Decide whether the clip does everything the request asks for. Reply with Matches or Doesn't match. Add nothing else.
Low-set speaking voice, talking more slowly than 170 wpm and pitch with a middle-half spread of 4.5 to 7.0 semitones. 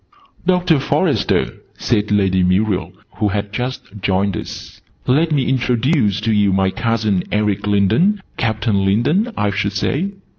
Matches